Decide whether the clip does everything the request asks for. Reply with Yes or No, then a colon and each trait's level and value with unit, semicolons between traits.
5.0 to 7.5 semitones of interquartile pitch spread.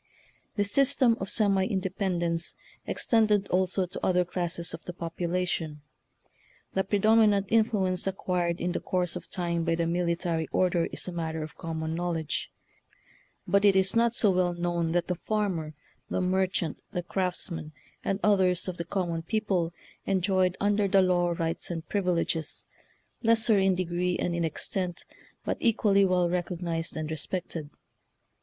No: narrow, 2.4 semitones